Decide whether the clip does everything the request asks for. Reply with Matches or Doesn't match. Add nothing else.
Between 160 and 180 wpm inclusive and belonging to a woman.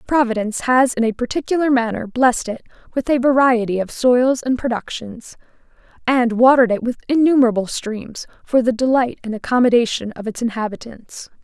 Doesn't match